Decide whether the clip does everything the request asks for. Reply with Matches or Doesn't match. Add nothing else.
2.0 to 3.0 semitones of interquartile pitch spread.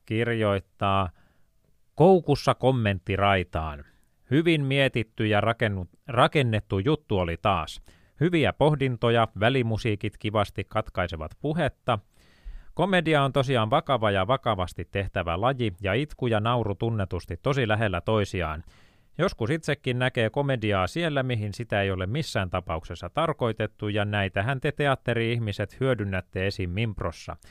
Doesn't match